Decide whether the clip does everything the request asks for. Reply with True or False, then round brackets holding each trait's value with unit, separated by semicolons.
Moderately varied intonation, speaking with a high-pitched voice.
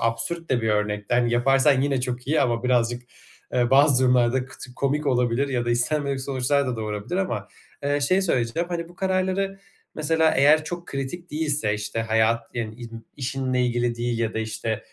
False (4.0 semitones; 125 Hz)